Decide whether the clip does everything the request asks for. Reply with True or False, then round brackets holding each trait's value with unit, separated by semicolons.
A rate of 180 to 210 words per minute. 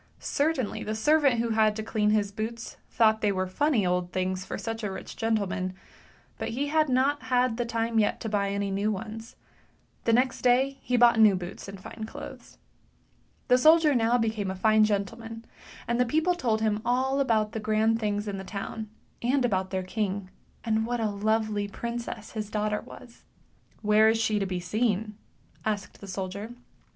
True (190 wpm)